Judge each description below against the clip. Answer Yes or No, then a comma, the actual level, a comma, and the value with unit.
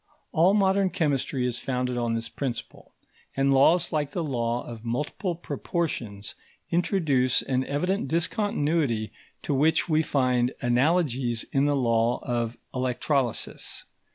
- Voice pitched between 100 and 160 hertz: Yes, low, 135 Hz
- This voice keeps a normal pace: No, slow, 125 wpm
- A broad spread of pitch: No, average, 4.9 semitones